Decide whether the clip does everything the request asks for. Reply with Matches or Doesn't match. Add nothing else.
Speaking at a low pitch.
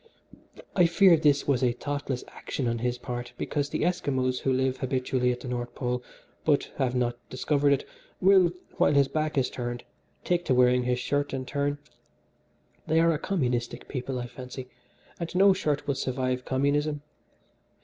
Matches